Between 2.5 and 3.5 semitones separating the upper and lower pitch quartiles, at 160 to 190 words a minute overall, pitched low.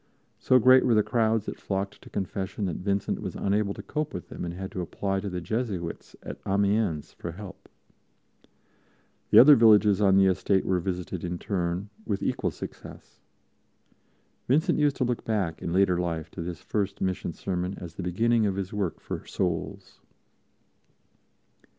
Yes: average, 3.1 semitones; average, 170 wpm; very low, 95 Hz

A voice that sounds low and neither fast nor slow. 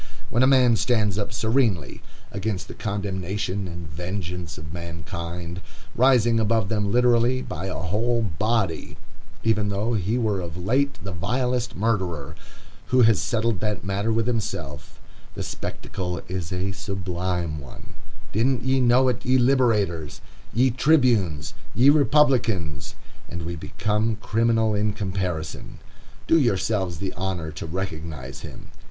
No: low, 100 Hz; slow, 130 wpm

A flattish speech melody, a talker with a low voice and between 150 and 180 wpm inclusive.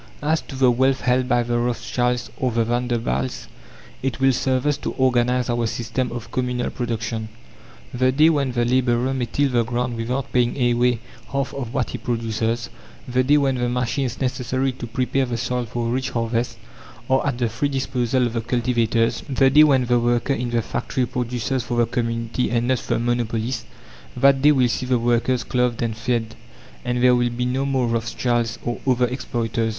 No: narrow, 1.6 semitones; low, 125 Hz; average, 190 wpm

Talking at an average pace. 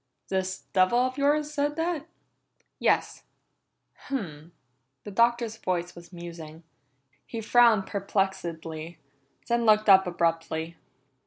No: slow, 105 wpm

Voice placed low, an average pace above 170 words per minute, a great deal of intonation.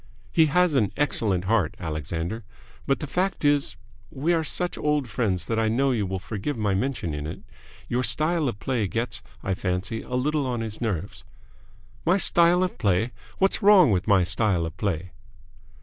Yes: low, 115 Hz; average, 180 wpm; wide, 7.4 semitones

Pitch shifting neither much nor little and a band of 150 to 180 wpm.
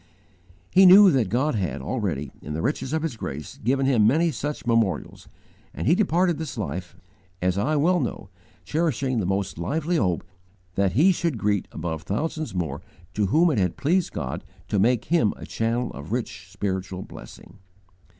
No: wide, 8.6 semitones; average, 175 wpm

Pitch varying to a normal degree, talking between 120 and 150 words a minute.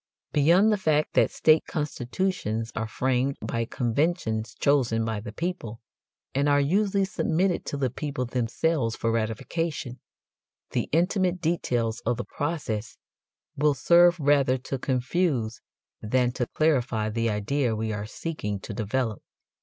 No: wide, 5.9 semitones; average, 140 wpm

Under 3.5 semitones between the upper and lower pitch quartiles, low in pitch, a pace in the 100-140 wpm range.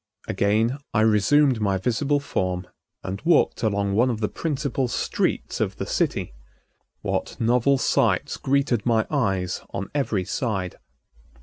No: average, 5.3 semitones; low, 115 Hz; slow, 135 wpm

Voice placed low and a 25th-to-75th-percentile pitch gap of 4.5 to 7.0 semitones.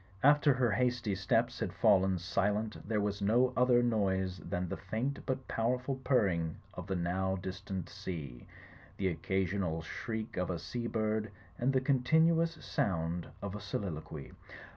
Yes: low, 100 Hz; average, 4.9 semitones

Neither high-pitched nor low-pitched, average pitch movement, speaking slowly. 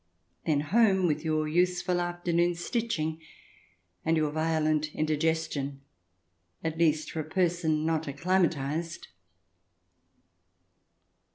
No: medium, 160 Hz; narrow, 2.2 semitones; slow, 100 wpm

